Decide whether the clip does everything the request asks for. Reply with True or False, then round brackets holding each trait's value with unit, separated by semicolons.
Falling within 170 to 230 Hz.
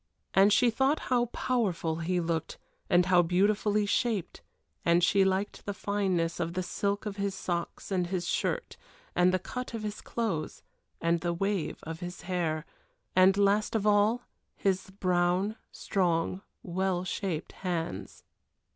True (190 Hz)